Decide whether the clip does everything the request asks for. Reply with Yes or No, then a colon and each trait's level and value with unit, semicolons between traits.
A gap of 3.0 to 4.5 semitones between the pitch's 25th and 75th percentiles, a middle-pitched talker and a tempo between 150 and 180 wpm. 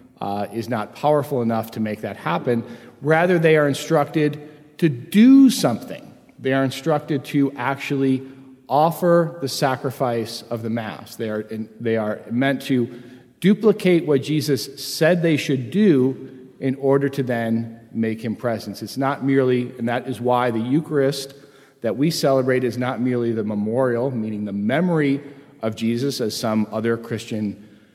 No: average, 3.7 semitones; low, 130 Hz; average, 160 wpm